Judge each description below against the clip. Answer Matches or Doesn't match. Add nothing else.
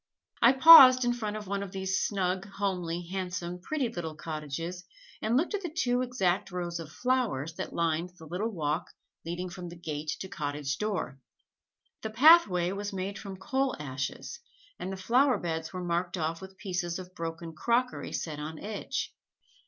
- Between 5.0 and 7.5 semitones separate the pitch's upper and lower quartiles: Doesn't match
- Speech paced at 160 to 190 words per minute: Matches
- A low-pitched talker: Doesn't match